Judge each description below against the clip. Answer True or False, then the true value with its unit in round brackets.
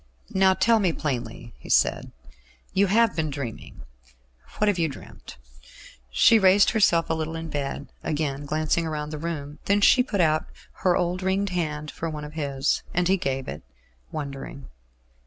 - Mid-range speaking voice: True (160 Hz)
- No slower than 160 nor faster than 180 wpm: True (170 wpm)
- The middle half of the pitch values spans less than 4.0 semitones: False (4.5 semitones)